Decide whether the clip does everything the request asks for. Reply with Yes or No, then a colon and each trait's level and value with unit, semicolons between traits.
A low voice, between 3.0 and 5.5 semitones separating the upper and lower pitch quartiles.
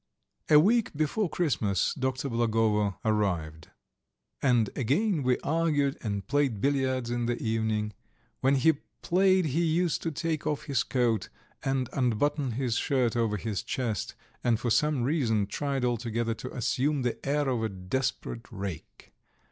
Yes: low, 125 Hz; average, 4.5 semitones